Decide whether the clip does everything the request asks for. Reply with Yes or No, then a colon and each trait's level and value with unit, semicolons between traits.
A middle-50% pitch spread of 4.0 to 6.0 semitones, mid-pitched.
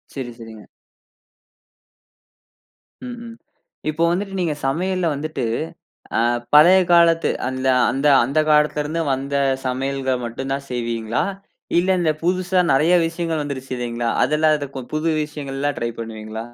Yes: average, 4.4 semitones; medium, 145 Hz